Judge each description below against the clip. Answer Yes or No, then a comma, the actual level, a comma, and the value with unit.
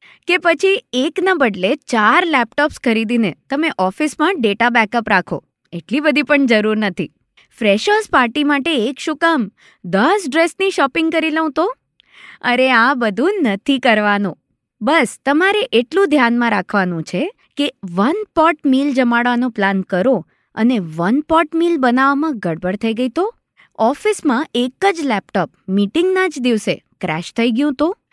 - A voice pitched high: Yes, very high, 260 Hz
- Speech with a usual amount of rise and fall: No, wide, 6.9 semitones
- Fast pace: Yes, fast, 145 wpm